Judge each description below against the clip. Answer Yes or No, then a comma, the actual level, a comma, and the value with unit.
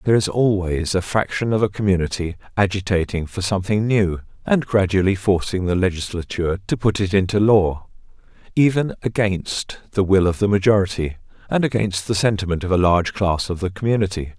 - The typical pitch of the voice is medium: No, low, 100 Hz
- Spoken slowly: No, average, 165 wpm